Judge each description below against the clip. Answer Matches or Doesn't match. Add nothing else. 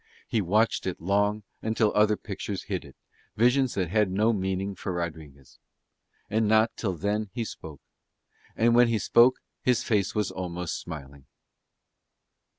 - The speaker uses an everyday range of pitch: Matches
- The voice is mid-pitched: Doesn't match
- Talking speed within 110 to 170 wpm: Matches